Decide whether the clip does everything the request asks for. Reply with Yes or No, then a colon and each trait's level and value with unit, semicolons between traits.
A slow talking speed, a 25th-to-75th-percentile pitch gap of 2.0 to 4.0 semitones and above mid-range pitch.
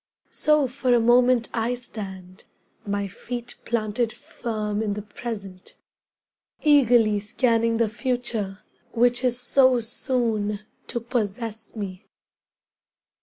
Yes: slow, 110 wpm; average, 2.8 semitones; high, 230 Hz